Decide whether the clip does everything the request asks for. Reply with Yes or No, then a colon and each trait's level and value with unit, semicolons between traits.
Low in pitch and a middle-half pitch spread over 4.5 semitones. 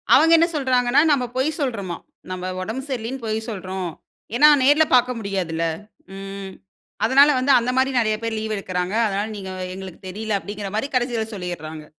No: high, 215 Hz; average, 5.0 semitones